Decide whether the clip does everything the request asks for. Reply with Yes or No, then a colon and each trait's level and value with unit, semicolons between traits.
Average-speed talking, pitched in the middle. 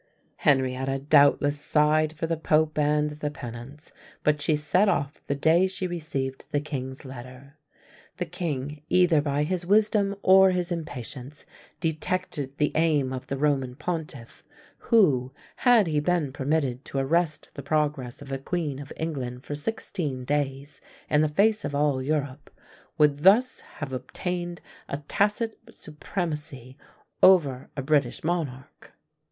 Yes: average, 145 wpm; medium, 150 Hz